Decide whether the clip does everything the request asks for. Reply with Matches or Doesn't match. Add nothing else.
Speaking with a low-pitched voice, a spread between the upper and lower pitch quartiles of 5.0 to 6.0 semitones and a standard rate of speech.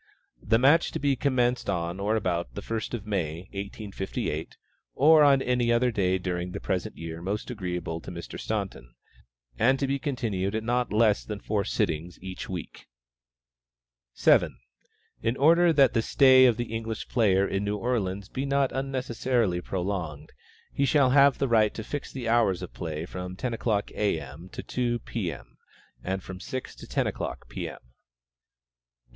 Matches